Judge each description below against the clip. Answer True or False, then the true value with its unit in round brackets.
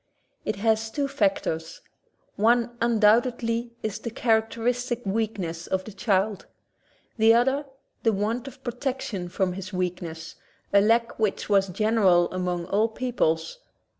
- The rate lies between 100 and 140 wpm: True (135 wpm)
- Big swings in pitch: False (3.9 semitones)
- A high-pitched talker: True (220 Hz)